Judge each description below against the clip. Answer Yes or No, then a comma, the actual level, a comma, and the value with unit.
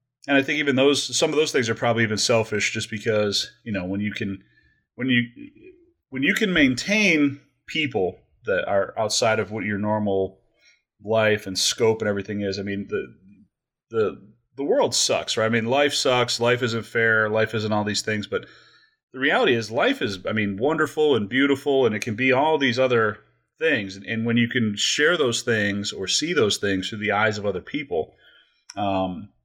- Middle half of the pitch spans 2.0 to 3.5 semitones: No, average, 3.9 semitones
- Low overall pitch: Yes, low, 110 Hz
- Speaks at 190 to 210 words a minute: Yes, average, 200 wpm